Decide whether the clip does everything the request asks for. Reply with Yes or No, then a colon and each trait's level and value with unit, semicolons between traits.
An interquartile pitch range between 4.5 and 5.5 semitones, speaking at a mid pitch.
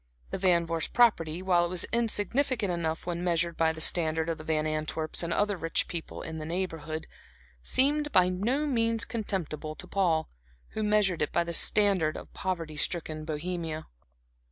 No: average, 4.0 semitones; medium, 170 Hz